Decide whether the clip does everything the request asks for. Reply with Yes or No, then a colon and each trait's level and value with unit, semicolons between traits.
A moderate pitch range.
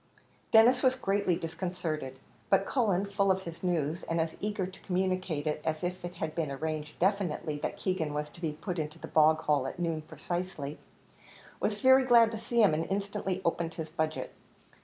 Yes: average, 3.9 semitones